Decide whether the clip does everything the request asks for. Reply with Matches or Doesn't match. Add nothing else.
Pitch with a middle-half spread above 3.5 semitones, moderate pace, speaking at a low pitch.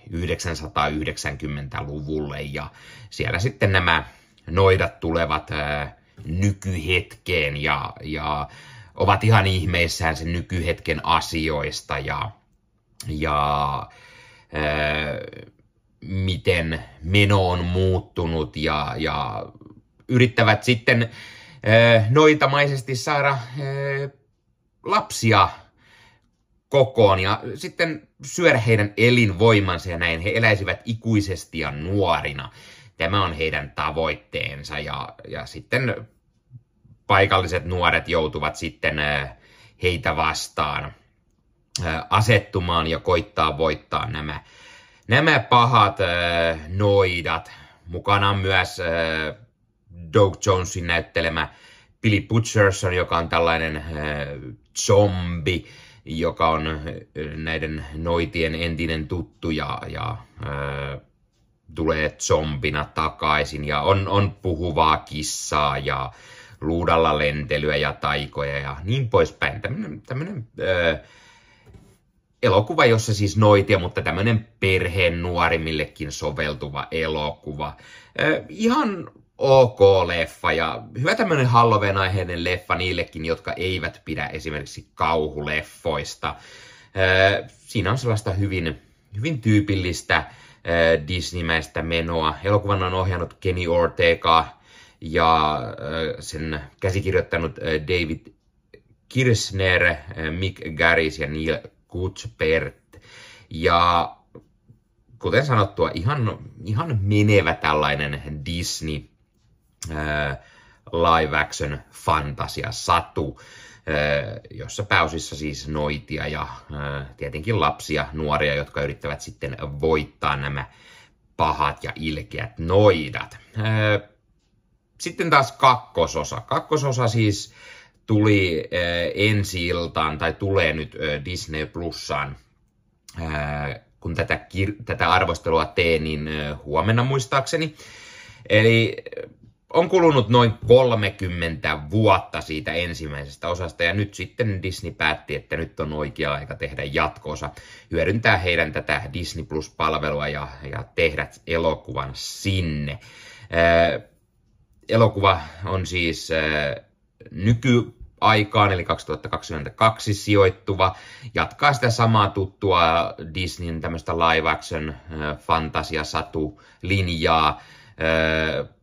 Doesn't match